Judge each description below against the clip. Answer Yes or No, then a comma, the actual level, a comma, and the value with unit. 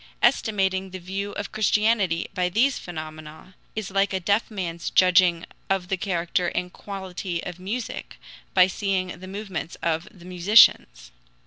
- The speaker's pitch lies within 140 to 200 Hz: Yes, medium, 185 Hz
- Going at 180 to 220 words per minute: No, average, 145 wpm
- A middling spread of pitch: No, narrow, 2.3 semitones